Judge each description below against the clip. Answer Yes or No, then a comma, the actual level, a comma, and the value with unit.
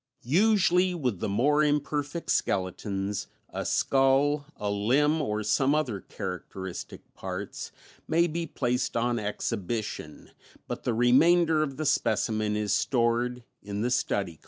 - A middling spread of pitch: No, wide, 6.3 semitones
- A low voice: Yes, low, 125 Hz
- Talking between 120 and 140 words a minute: Yes, slow, 135 wpm